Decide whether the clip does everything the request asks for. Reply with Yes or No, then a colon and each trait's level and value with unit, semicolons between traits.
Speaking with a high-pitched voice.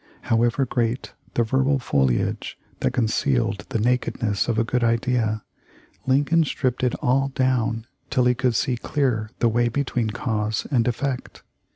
No: low, 120 Hz